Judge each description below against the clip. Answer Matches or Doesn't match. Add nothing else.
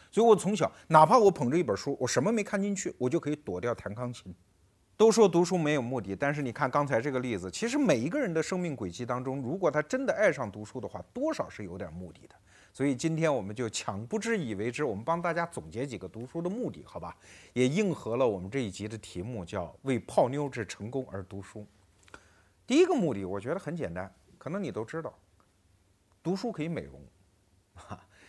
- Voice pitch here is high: Doesn't match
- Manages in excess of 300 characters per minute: Matches